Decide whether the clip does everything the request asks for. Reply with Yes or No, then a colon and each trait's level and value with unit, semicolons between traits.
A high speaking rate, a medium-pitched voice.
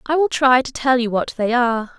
No: fast, 270 wpm; very high, 250 Hz